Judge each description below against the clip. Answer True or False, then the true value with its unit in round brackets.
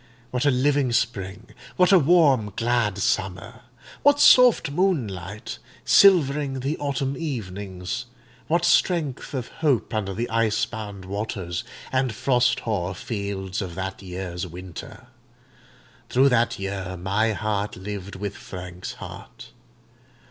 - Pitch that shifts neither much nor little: False (6.0 semitones)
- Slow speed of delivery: True (115 wpm)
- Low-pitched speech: True (110 Hz)